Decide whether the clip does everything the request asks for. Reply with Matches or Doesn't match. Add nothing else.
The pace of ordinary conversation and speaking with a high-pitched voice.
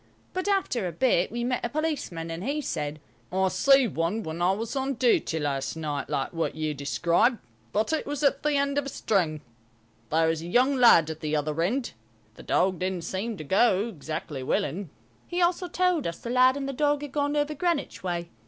Doesn't match